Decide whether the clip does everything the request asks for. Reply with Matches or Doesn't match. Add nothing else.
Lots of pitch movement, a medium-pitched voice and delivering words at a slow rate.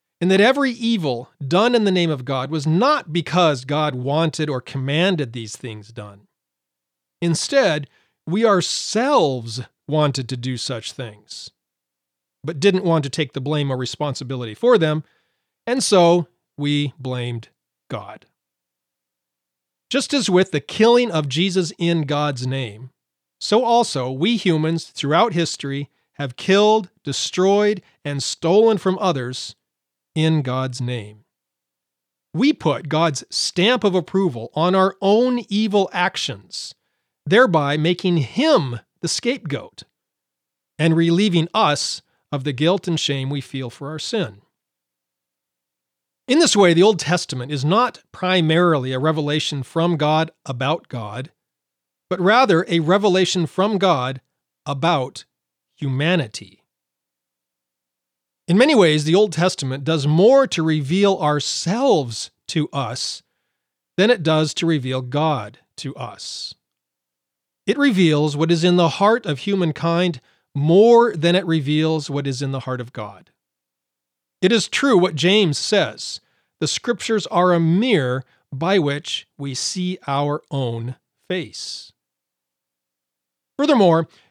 Matches